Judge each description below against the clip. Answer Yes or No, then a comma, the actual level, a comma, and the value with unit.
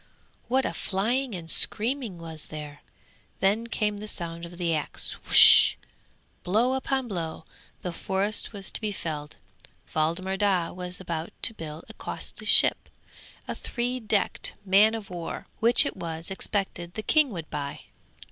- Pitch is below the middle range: No, high, 190 Hz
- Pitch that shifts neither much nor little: Yes, average, 4.7 semitones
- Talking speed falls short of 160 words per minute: Yes, average, 150 wpm